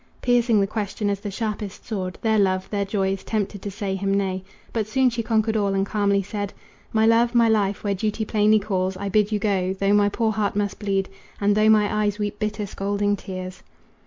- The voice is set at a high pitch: Yes, high, 205 Hz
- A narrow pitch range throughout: Yes, narrow, 1.7 semitones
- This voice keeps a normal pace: No, fast, 215 wpm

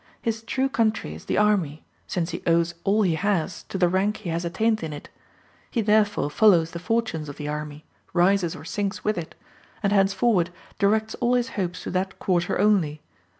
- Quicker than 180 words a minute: Yes, average, 195 wpm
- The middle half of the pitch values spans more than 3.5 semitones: Yes, average, 4.2 semitones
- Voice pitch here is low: No, high, 190 Hz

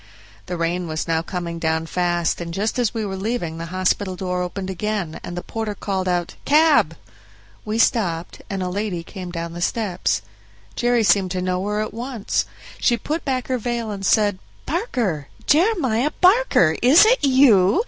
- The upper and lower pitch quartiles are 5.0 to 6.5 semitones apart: Yes, wide, 5.4 semitones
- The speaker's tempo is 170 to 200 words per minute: Yes, average, 180 wpm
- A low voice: No, high, 195 Hz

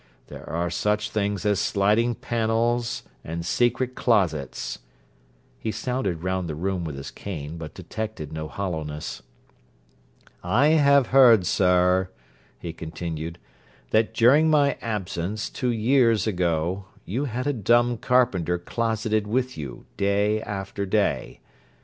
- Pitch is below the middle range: Yes, low, 105 Hz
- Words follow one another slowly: Yes, slow, 125 wpm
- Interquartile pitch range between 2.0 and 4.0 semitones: No, average, 5.2 semitones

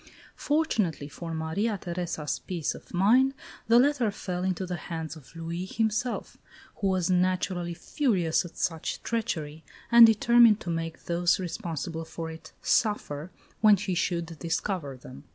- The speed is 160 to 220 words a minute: No, average, 145 wpm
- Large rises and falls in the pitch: No, average, 4.5 semitones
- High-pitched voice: No, medium, 180 Hz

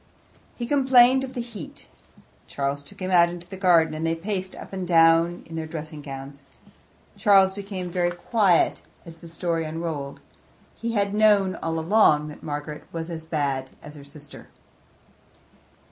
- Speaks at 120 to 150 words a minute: No, average, 160 wpm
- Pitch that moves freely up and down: No, average, 4.1 semitones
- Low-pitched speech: No, medium, 170 Hz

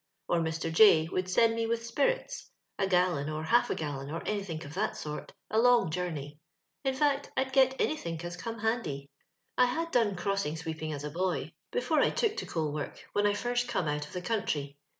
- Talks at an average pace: No, fast, 215 wpm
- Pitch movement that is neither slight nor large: No, wide, 6.7 semitones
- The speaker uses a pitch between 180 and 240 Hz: Yes, medium, 185 Hz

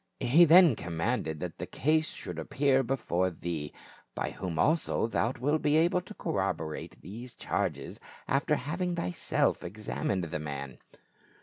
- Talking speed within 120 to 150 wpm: Yes, average, 140 wpm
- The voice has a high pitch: No, low, 110 Hz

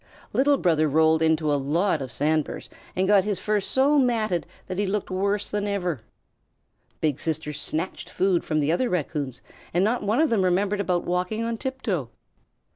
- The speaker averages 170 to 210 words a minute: Yes, average, 180 wpm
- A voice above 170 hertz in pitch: Yes, medium, 185 Hz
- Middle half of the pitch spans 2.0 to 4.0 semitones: No, average, 4.8 semitones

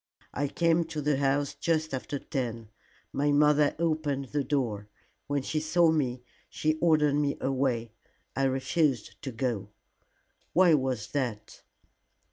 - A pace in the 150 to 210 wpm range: No, slow, 135 wpm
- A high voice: No, medium, 140 Hz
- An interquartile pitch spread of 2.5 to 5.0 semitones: Yes, average, 3.0 semitones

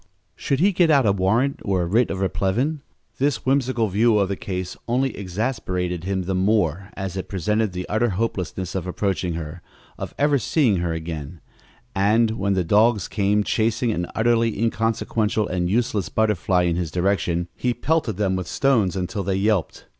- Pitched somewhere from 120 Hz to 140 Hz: No, low, 100 Hz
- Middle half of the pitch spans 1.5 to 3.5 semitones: No, average, 4.0 semitones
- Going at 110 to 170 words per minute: No, average, 180 wpm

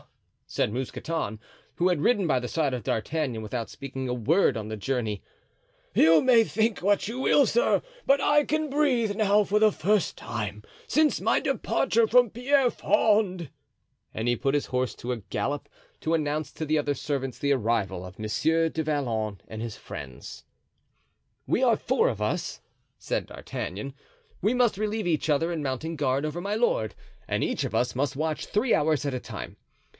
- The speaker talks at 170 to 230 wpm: Yes, average, 180 wpm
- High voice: No, medium, 155 Hz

